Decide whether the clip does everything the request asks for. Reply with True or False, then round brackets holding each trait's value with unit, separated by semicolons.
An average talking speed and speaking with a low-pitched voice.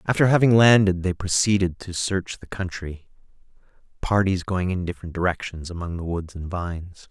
True (160 wpm; 90 Hz)